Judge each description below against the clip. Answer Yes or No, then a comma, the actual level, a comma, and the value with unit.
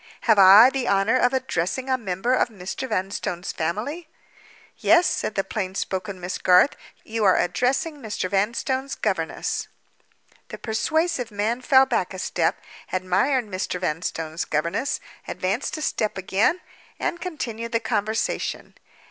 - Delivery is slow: Yes, slow, 130 wpm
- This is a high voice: Yes, high, 220 Hz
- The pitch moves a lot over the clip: Yes, wide, 5.8 semitones